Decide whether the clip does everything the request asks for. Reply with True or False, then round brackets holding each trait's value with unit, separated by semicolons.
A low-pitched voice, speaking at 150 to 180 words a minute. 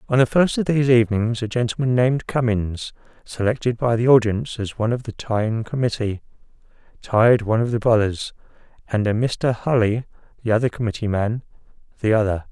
True (115 Hz; 170 wpm)